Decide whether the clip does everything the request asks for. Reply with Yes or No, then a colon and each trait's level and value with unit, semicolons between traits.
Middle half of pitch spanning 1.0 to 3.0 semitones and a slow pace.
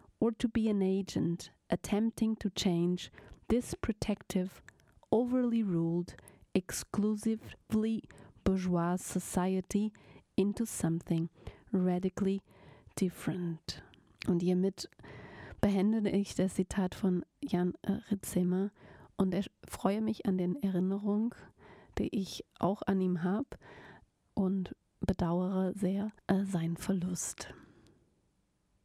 Yes: narrow, 2.5 semitones; slow, 100 wpm